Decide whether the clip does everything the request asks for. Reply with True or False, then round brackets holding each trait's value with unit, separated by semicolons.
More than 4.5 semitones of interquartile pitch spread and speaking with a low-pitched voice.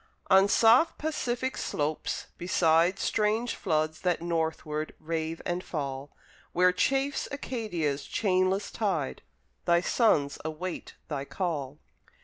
False (5.2 semitones; 175 Hz)